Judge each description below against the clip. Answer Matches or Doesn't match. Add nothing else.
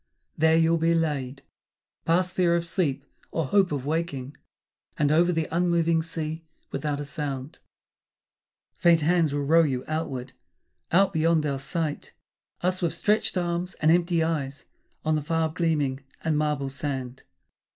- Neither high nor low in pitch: Matches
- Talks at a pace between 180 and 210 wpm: Doesn't match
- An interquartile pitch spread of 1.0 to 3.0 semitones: Matches